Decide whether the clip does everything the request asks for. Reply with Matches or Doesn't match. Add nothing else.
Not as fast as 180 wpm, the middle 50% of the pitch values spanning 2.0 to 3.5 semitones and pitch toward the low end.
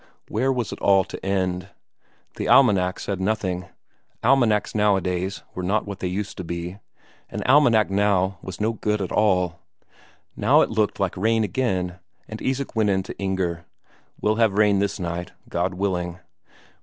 Matches